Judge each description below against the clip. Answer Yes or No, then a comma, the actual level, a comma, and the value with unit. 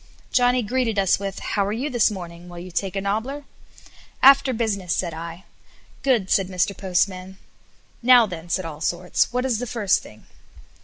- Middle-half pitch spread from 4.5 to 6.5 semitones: Yes, average, 5.2 semitones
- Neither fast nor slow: Yes, average, 170 wpm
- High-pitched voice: Yes, high, 200 Hz